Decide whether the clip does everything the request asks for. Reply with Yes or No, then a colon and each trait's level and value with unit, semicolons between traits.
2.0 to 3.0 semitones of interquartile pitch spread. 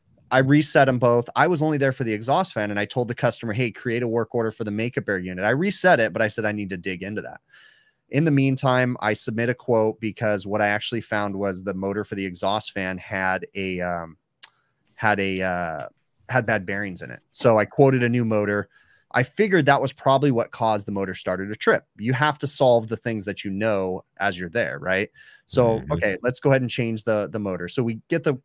No: average, 4.1 semitones